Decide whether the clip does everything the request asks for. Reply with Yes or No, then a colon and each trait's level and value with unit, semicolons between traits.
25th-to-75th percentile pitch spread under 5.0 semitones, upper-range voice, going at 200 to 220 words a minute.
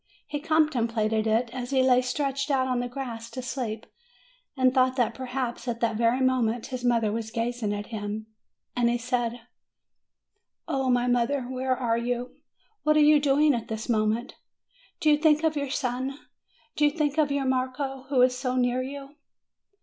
No: narrow, 2.6 semitones; very high, 255 Hz; average, 185 wpm